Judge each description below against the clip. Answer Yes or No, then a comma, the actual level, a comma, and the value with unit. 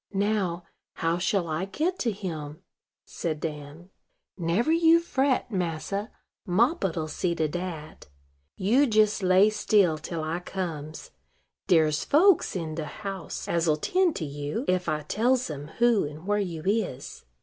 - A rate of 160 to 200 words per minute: No, average, 145 wpm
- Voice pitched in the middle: Yes, medium, 180 Hz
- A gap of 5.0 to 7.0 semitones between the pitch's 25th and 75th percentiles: Yes, average, 5.3 semitones